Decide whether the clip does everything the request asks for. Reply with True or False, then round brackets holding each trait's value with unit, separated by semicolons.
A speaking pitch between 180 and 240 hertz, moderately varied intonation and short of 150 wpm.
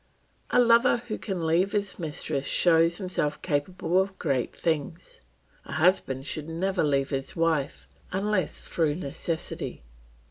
False (165 Hz; 4.3 semitones; 135 wpm)